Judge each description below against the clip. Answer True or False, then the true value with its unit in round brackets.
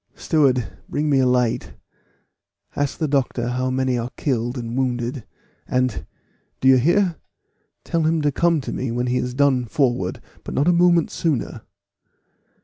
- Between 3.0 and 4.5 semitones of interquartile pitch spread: True (3.3 semitones)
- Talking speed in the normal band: True (160 wpm)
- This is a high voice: False (130 Hz)